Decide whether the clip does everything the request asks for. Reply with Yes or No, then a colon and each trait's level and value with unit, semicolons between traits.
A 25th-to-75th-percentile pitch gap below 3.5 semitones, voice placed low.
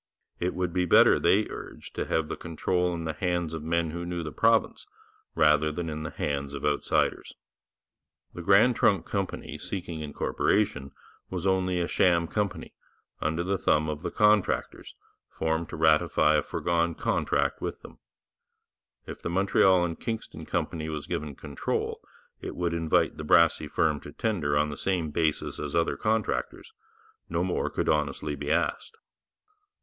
Yes: average, 3.0 semitones; very low, 85 Hz